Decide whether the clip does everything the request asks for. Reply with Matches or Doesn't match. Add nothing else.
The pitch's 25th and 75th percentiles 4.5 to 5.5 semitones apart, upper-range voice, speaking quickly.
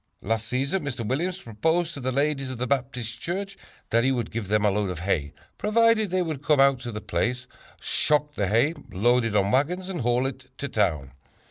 Doesn't match